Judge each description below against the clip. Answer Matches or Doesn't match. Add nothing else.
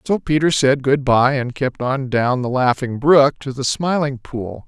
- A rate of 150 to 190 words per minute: Doesn't match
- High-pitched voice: Doesn't match